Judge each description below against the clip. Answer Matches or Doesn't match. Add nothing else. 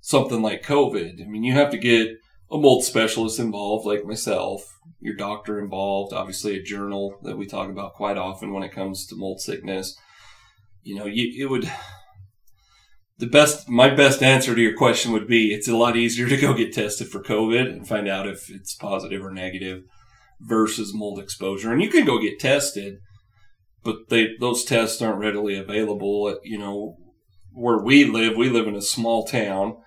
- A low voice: Matches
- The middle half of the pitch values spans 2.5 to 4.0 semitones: Matches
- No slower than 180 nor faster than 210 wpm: Matches